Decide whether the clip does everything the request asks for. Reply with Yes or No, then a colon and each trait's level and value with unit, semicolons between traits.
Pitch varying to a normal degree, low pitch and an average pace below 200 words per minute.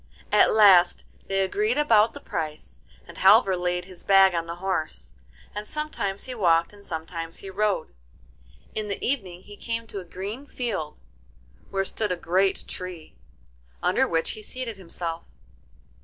No: average, 3.4 semitones; high, 195 Hz; average, 155 wpm